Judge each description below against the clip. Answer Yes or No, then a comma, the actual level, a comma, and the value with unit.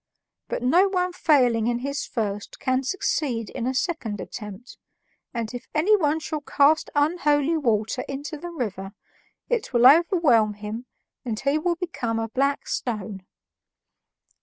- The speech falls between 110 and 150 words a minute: Yes, average, 140 wpm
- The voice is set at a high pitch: Yes, very high, 265 Hz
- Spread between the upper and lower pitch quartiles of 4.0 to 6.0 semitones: Yes, wide, 5.6 semitones